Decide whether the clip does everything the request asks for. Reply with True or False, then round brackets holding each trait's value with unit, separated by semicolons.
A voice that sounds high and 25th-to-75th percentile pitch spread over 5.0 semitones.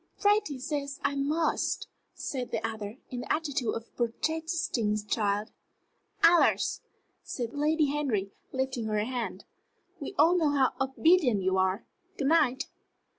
True (265 Hz; 5.4 semitones)